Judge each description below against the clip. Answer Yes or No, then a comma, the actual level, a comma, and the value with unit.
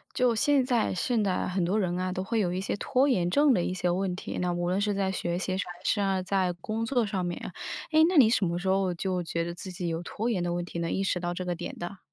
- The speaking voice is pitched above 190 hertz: No, medium, 185 Hz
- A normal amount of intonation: Yes, average, 3.3 semitones